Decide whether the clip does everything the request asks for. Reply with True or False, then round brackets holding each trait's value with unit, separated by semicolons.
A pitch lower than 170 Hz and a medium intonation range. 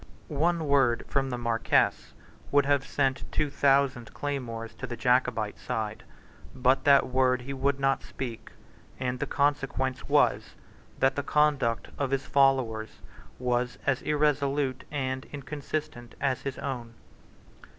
False (135 Hz; 2.3 semitones)